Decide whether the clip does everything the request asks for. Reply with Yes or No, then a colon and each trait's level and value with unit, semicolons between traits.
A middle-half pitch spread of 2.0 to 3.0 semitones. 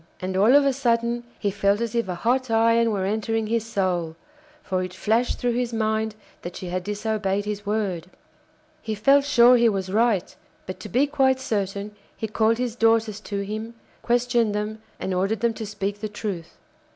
Yes: average, 2.7 semitones